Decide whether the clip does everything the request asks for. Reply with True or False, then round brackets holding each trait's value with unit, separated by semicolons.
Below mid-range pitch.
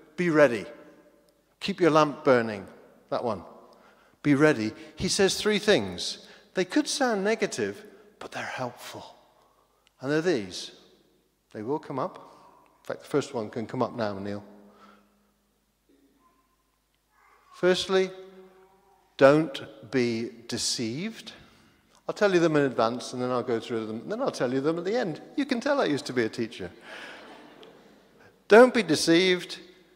False (155 Hz)